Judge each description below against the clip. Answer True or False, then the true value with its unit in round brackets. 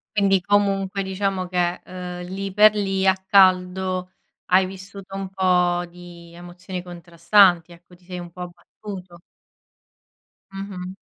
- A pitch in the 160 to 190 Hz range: True (185 Hz)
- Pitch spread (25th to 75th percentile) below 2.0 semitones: True (1.6 semitones)